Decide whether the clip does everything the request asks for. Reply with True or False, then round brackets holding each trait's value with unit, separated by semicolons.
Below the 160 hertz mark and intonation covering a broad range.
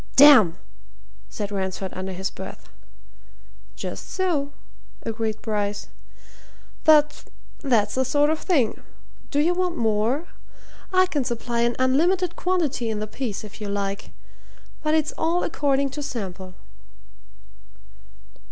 False (260 Hz; 6.5 semitones)